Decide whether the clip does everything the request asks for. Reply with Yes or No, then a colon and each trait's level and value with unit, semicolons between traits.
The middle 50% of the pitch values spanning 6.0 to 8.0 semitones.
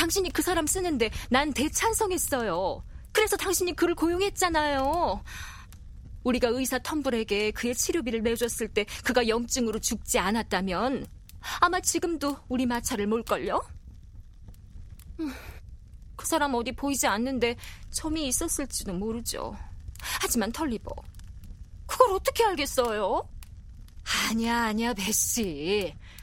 Yes: wide, 6.4 semitones